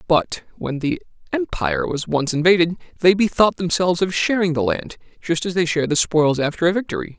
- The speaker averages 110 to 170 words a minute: No, average, 185 wpm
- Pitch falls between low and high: Yes, medium, 170 Hz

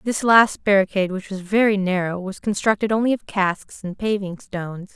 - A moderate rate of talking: Yes, average, 180 wpm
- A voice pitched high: Yes, high, 200 Hz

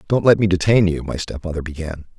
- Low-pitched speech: Yes, very low, 90 Hz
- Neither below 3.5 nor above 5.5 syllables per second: No, 6.2 syllables/s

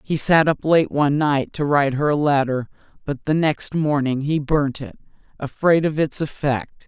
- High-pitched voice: No, medium, 145 Hz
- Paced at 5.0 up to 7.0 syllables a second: No, 4.8 syllables/s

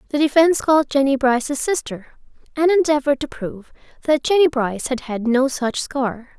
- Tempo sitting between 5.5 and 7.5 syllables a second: Yes, 5.6 syllables/s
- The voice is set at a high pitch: Yes, very high, 275 Hz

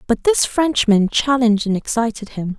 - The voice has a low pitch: No, high, 235 Hz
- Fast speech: No, average, 165 wpm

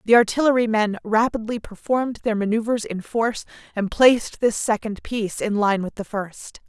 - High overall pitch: Yes, high, 220 Hz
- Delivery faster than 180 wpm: No, average, 170 wpm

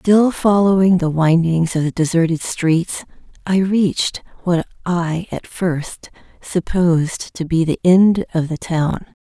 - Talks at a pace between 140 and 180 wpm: Yes, average, 145 wpm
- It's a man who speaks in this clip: No, female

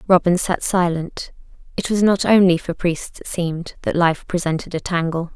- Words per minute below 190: Yes, average, 180 wpm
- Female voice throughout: Yes, female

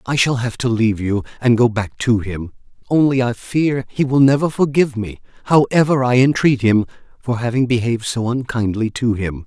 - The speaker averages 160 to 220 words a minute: Yes, average, 190 wpm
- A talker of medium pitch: No, low, 120 Hz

